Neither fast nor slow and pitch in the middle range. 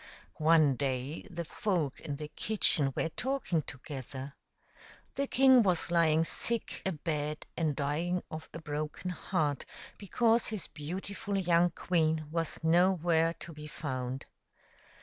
No: slow, 130 wpm; medium, 165 Hz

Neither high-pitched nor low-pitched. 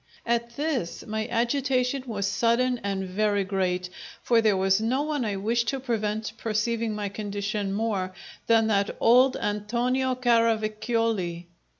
No: high, 220 Hz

